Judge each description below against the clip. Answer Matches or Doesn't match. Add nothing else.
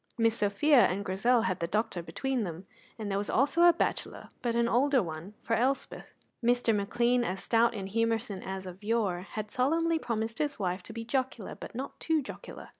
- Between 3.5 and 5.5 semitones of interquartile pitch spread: Matches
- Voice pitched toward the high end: Matches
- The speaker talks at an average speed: Matches